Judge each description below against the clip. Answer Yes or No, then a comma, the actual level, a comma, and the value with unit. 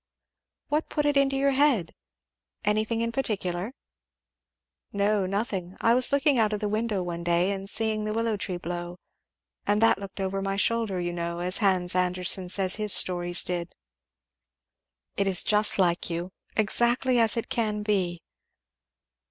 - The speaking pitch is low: No, high, 200 Hz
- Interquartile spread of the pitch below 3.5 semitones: No, average, 4.0 semitones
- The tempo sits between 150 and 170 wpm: Yes, average, 160 wpm